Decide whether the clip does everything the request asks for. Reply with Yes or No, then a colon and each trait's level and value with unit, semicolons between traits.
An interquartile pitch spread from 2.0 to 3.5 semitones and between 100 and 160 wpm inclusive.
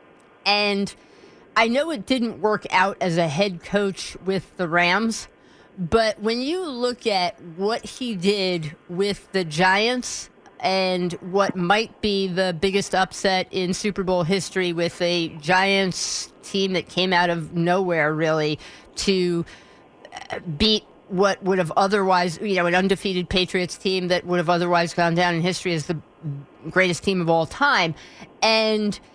Yes: narrow, 2.4 semitones; average, 150 wpm